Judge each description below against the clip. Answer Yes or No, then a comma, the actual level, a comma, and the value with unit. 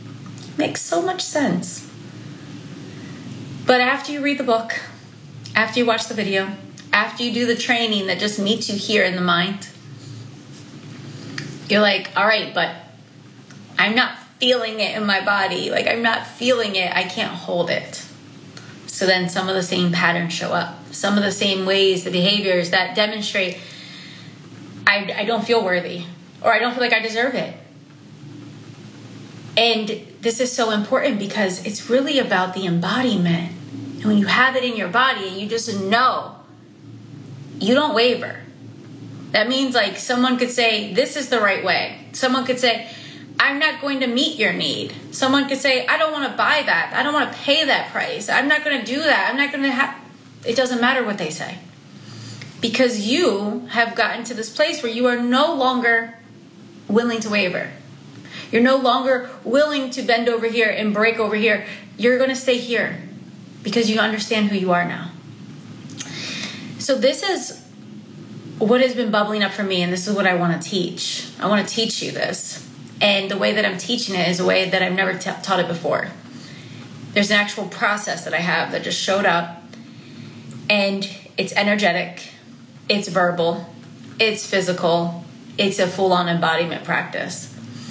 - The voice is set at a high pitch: Yes, high, 210 Hz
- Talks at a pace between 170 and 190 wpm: Yes, average, 180 wpm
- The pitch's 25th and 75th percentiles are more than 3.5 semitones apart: Yes, average, 5.0 semitones